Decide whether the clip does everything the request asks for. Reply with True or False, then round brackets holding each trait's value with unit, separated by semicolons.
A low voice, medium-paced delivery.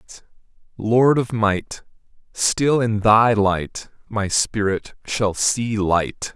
False (110 Hz; 125 wpm)